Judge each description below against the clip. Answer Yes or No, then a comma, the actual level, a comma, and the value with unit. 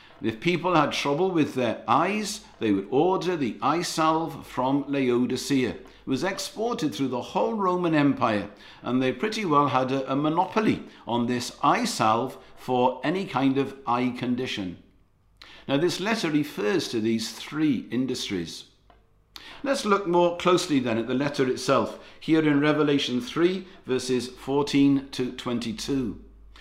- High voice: No, medium, 140 Hz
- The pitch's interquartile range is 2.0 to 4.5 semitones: No, wide, 5.6 semitones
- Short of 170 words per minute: Yes, average, 145 wpm